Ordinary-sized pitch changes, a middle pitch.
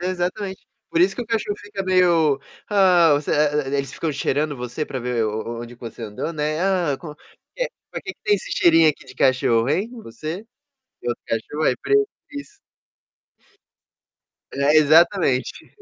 No: wide, 6.1 semitones; medium, 155 Hz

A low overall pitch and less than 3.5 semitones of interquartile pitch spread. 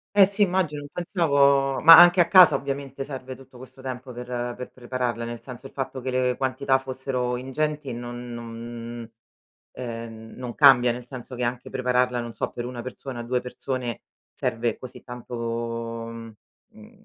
Yes: low, 125 Hz; narrow, 2.4 semitones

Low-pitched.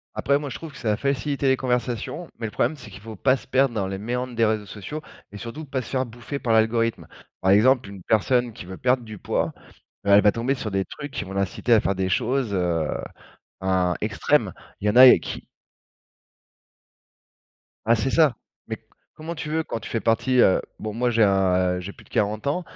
Yes: low, 115 Hz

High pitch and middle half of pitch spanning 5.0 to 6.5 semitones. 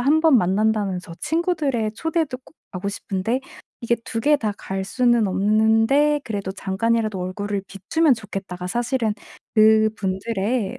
No: high, 220 Hz; average, 4.4 semitones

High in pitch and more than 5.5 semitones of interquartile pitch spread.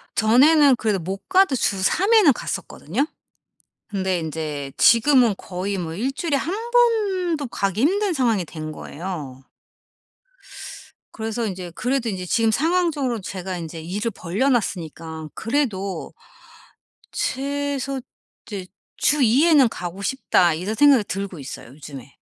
Yes: high, 220 Hz; wide, 7.7 semitones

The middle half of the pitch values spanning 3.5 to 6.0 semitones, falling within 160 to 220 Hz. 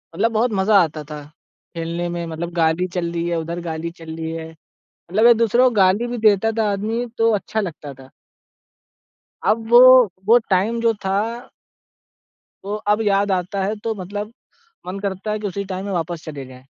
Yes: average, 4.3 semitones; high, 190 Hz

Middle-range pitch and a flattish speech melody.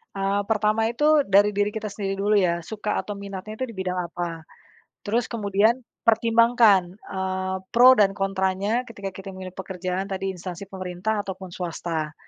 No: high, 195 Hz; narrow, 2.3 semitones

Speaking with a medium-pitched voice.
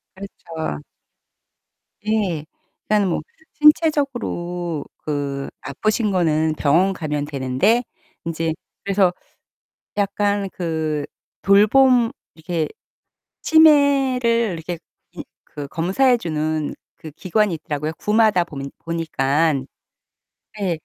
Yes: medium, 175 Hz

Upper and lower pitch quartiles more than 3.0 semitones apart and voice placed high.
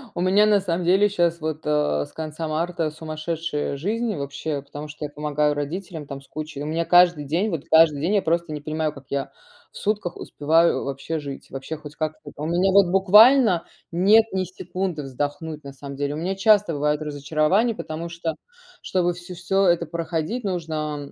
No: average, 3.4 semitones; medium, 160 Hz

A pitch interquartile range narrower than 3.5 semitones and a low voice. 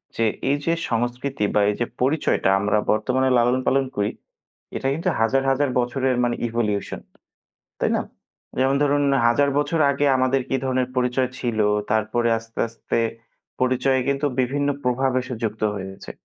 Yes: average, 2.8 semitones; low, 125 Hz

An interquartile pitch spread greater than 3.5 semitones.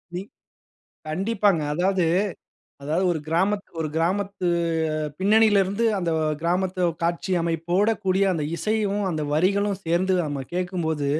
No: average, 3.1 semitones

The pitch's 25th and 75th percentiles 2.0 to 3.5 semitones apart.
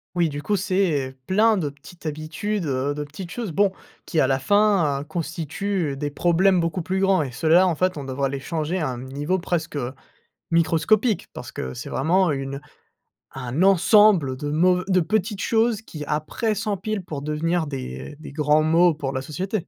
No: average, 4.7 semitones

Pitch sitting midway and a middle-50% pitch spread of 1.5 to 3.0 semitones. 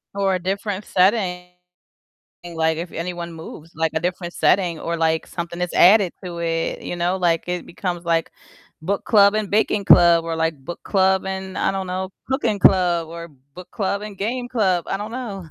Yes: medium, 180 Hz; average, 2.7 semitones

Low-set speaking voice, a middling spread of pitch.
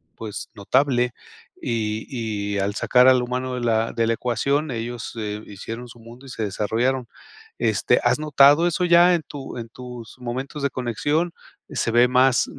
Yes: low, 125 Hz; average, 3.0 semitones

